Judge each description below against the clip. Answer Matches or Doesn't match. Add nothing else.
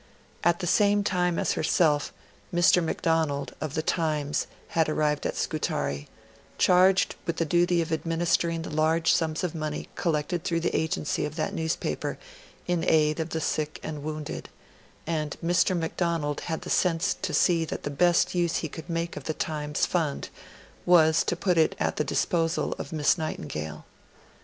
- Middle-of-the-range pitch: Matches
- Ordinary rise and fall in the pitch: Doesn't match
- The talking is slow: Doesn't match